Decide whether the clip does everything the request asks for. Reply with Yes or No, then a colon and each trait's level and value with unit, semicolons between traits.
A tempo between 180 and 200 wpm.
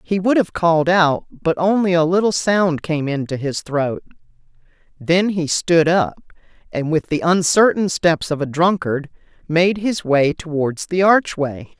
No: average, 165 wpm